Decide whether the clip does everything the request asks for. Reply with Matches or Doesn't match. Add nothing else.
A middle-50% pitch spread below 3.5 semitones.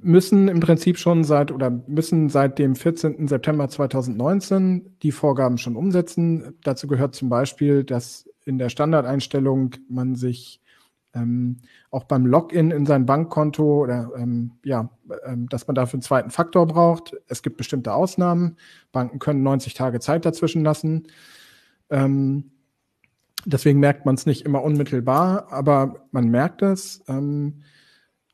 Doesn't match